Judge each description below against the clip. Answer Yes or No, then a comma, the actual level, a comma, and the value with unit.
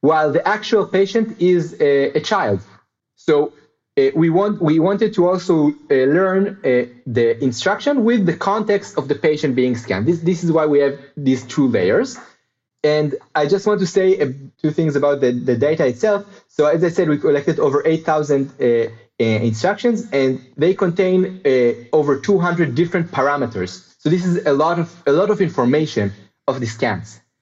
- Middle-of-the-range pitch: Yes, medium, 155 Hz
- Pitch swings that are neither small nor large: No, wide, 6.1 semitones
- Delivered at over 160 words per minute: Yes, average, 185 wpm